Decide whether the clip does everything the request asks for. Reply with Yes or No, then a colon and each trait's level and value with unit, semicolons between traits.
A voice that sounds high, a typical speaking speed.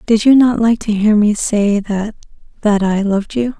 Yes: high, 215 Hz; average, 185 wpm